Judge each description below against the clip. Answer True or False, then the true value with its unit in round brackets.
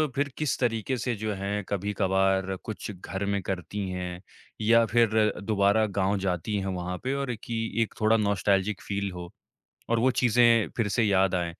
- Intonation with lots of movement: False (3.0 semitones)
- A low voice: True (100 Hz)